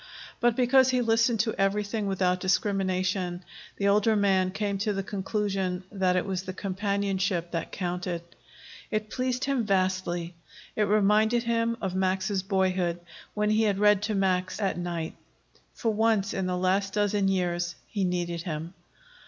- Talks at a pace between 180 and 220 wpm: No, average, 155 wpm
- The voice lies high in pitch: Yes, high, 195 Hz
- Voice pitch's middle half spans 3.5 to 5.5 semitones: No, narrow, 2.4 semitones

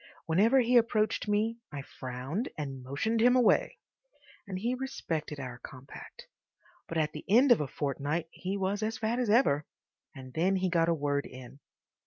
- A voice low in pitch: No, medium, 180 Hz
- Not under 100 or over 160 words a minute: No, average, 175 wpm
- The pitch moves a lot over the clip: Yes, wide, 7.9 semitones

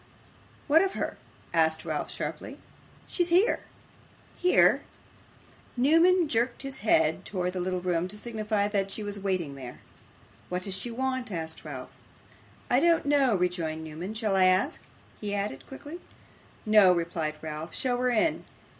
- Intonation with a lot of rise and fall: Yes, wide, 6.7 semitones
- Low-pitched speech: No, high, 200 Hz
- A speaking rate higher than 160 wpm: No, average, 150 wpm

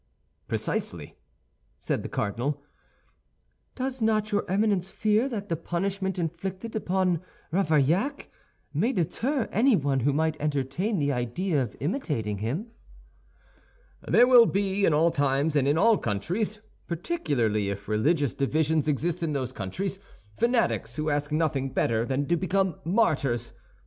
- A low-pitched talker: No, medium, 165 Hz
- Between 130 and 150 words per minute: Yes, slow, 135 wpm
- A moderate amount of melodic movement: No, wide, 6.2 semitones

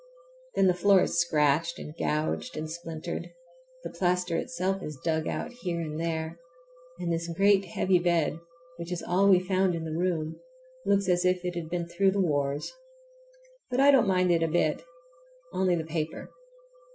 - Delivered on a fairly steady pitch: Yes, narrow, 2.2 semitones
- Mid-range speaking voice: Yes, medium, 170 Hz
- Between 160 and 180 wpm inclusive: Yes, average, 175 wpm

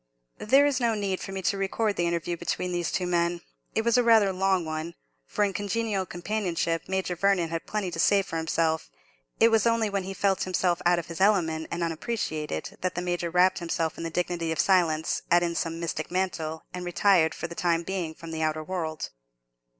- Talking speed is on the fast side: Yes, fast, 210 wpm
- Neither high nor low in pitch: Yes, medium, 175 Hz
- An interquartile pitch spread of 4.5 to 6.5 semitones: No, average, 2.9 semitones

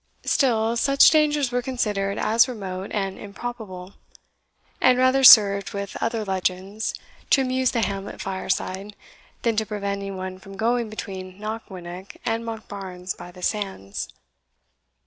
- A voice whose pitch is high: Yes, high, 205 Hz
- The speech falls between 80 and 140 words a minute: Yes, slow, 135 wpm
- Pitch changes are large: No, average, 3.3 semitones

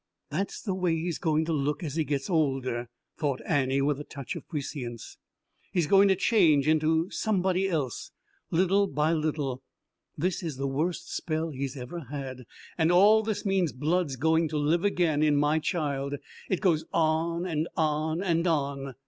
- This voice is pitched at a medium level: Yes, medium, 155 Hz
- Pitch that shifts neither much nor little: Yes, average, 3.6 semitones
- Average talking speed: Yes, average, 175 wpm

